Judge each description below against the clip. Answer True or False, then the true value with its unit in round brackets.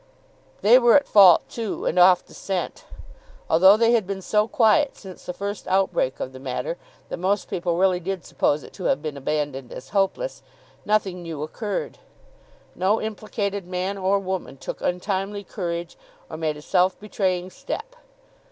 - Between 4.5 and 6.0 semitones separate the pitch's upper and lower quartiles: False (3.0 semitones)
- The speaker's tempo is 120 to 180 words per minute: True (170 wpm)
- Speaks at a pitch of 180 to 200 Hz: True (190 Hz)